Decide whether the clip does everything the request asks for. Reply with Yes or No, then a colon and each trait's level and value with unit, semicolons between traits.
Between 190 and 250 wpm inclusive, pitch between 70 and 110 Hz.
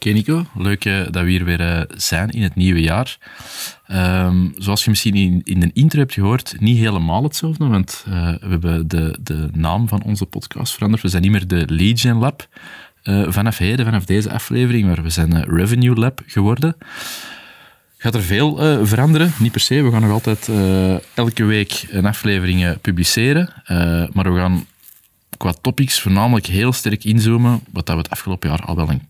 Yes: average, 195 wpm; low, 100 Hz